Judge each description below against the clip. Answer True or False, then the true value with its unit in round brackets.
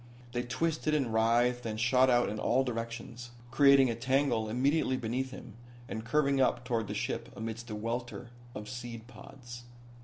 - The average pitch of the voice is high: False (120 Hz)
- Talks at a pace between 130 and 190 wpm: True (165 wpm)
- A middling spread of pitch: False (2.3 semitones)